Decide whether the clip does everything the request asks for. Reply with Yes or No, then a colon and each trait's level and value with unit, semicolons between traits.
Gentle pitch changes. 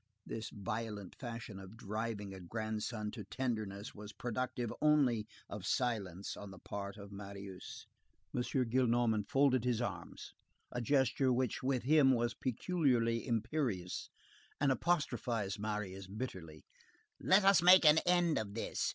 No: average, 4.1 semitones